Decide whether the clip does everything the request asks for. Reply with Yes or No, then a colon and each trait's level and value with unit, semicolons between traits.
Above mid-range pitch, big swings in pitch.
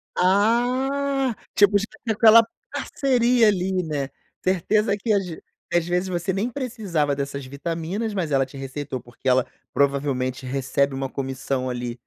No: medium, 170 Hz; wide, 8.1 semitones